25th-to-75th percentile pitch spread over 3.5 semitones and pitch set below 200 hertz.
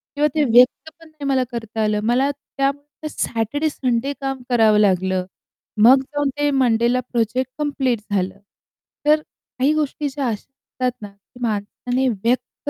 No: average, 4.1 semitones; very high, 255 Hz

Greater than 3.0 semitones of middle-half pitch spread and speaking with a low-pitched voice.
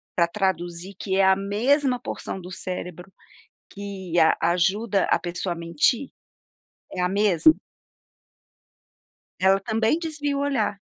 No: average, 3.9 semitones; high, 195 Hz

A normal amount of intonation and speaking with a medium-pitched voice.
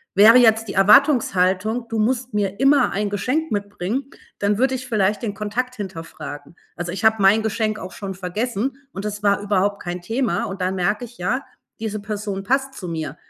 No: average, 3.5 semitones; high, 210 Hz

